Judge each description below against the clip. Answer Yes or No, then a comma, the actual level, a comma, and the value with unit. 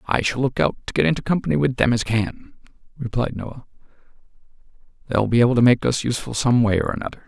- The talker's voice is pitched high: No, low, 120 Hz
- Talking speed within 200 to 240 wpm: Yes, fast, 205 wpm